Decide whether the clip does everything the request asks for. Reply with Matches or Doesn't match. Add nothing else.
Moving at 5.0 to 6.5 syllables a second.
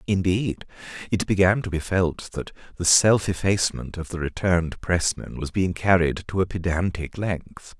Doesn't match